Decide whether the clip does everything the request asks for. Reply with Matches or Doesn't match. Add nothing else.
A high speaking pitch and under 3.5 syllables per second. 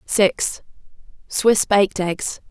Matches